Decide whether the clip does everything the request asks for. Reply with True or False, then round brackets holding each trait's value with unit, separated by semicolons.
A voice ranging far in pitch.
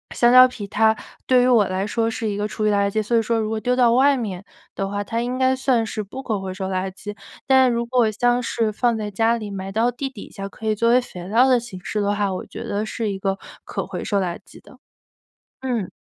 False (3.3 semitones)